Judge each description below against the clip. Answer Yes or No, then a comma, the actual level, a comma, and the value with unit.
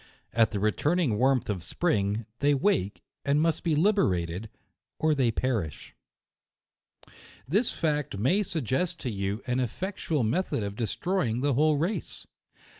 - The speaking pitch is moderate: No, low, 130 Hz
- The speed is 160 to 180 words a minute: No, average, 140 wpm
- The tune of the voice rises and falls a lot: Yes, wide, 7.1 semitones